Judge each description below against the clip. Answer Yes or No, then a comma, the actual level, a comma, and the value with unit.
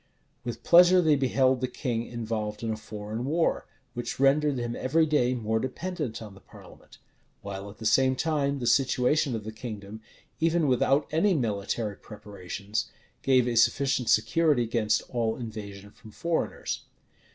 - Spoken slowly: No, average, 155 wpm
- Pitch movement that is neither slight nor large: Yes, average, 4.4 semitones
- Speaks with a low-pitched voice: Yes, low, 120 Hz